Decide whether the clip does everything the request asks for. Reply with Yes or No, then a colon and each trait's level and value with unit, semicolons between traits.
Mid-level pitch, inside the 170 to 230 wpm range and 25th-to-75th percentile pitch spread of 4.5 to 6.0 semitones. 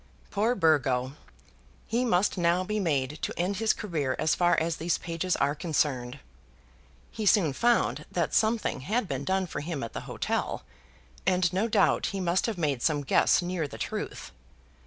Yes: medium, 175 Hz; average, 175 wpm; average, 5.2 semitones